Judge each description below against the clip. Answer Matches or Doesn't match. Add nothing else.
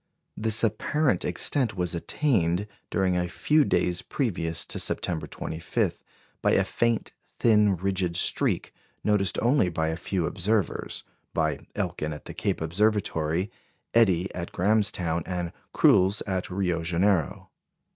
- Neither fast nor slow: Doesn't match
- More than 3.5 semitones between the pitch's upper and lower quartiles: Matches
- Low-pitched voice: Matches